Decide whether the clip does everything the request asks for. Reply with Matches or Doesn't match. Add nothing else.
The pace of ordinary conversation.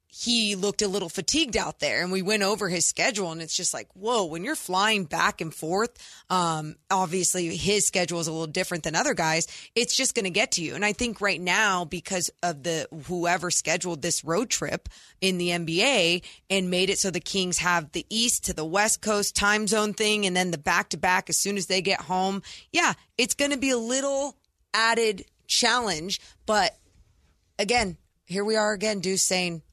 Doesn't match